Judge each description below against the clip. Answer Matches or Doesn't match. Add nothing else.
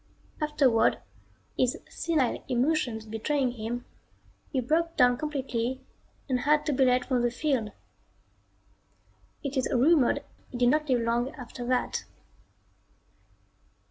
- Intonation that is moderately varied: Matches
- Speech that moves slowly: Matches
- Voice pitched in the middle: Doesn't match